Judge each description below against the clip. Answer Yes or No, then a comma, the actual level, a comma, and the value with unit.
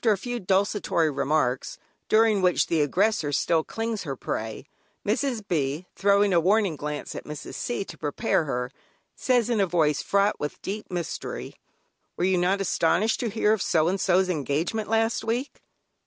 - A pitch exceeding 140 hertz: Yes, high, 190 Hz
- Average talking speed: Yes, average, 175 wpm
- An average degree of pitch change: No, wide, 5.8 semitones